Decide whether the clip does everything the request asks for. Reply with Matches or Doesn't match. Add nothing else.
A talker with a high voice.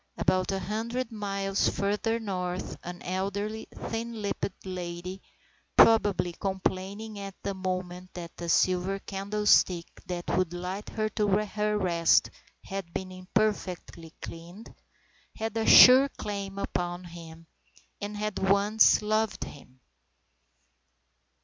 Matches